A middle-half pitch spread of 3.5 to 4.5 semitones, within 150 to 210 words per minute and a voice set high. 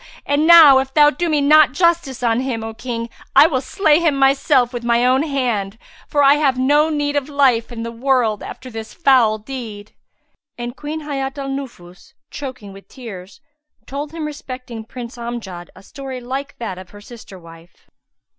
Yes: average, 3.9 semitones; average, 180 wpm; very high, 260 Hz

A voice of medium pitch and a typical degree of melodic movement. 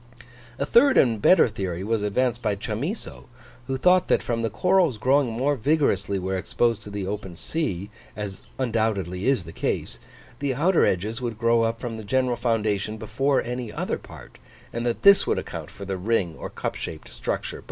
No: low, 115 Hz; average, 4.4 semitones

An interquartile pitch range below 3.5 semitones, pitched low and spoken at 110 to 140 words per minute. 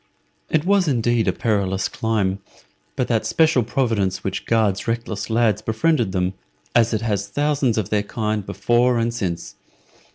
No: average, 2.9 semitones; low, 115 Hz; average, 155 wpm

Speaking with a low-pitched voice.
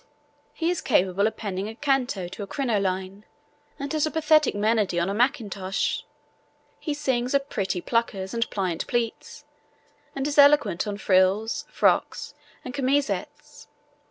No: high, 225 Hz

